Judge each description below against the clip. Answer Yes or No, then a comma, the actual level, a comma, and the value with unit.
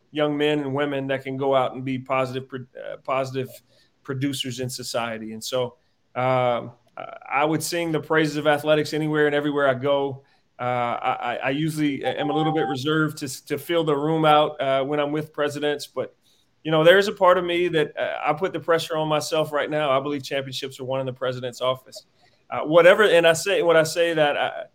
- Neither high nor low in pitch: Yes, medium, 145 Hz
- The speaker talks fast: Yes, fast, 215 wpm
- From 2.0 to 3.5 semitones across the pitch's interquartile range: Yes, average, 2.7 semitones